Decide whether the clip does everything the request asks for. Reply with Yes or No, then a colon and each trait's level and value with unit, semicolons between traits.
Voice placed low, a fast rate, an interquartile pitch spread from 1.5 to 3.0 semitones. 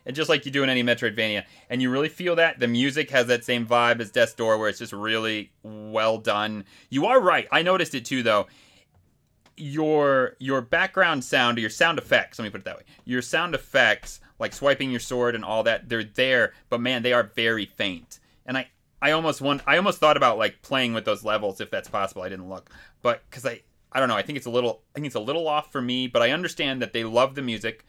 No: low, 125 Hz; fast, 245 wpm; average, 3.8 semitones